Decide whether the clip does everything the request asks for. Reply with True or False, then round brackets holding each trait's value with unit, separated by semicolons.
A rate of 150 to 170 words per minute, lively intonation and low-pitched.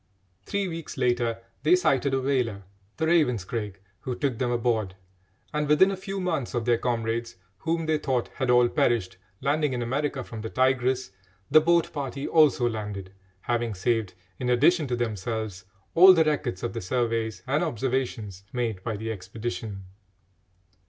False (160 wpm; 4.4 semitones; 125 Hz)